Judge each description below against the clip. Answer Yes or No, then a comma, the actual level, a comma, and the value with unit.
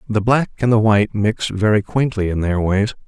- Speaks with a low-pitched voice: Yes, low, 105 Hz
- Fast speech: Yes, fast, 215 wpm